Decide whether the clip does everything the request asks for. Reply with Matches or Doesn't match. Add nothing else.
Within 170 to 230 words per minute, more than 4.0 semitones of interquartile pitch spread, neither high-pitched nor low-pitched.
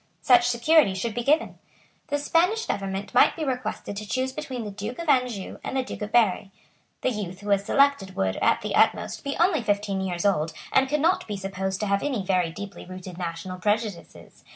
Doesn't match